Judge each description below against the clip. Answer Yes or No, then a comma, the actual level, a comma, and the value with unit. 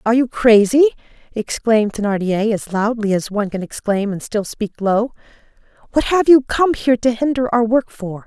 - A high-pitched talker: Yes, high, 225 Hz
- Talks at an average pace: Yes, average, 180 wpm